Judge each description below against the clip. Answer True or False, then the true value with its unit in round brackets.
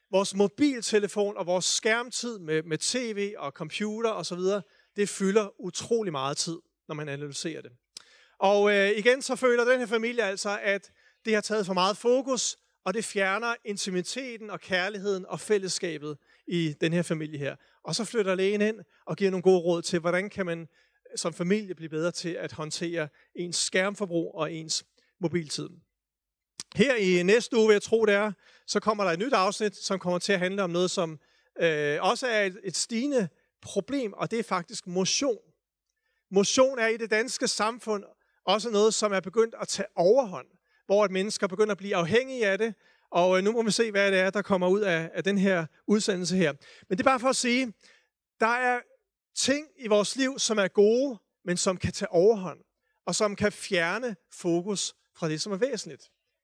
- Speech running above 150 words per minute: True (190 wpm)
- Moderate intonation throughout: True (3.9 semitones)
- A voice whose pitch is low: False (200 Hz)